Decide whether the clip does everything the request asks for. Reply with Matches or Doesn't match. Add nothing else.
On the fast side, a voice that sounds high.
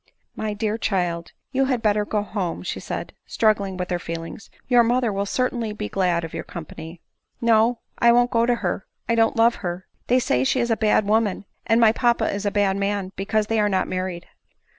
Matches